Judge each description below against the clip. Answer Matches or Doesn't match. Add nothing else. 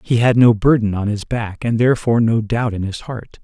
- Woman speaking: Doesn't match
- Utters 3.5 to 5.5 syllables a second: Matches